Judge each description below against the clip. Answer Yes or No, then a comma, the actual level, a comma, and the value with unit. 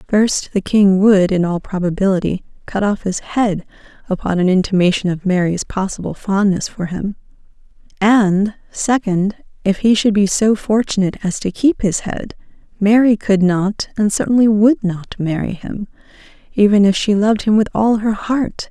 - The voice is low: No, high, 200 Hz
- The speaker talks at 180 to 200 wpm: No, average, 165 wpm